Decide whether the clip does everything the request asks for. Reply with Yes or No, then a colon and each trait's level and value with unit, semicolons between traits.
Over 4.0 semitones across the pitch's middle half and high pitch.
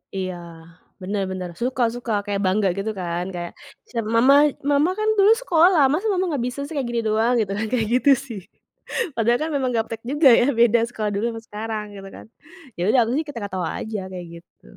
Yes: average, 4.7 semitones; high, 225 Hz